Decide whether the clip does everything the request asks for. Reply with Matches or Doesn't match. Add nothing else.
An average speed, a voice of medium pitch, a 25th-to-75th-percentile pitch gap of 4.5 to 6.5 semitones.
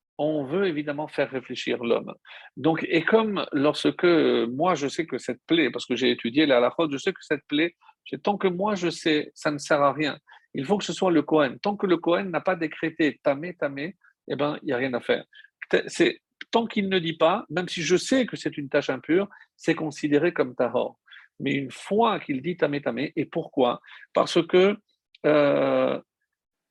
Matches